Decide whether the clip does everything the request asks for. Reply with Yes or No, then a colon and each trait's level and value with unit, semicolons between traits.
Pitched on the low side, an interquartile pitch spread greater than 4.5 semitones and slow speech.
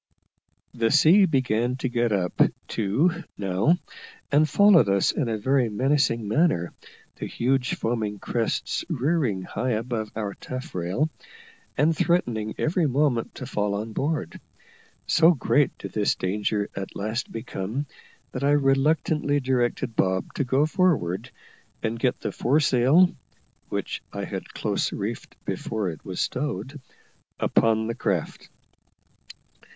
Yes: low, 125 Hz; wide, 5.4 semitones; slow, 130 wpm